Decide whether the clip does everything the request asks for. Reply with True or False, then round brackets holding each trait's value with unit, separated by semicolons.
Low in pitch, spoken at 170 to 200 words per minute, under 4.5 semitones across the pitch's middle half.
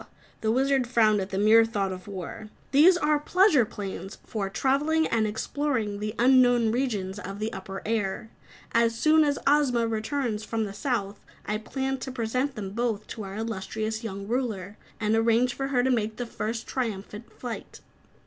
False (225 Hz; 175 wpm; 3.6 semitones)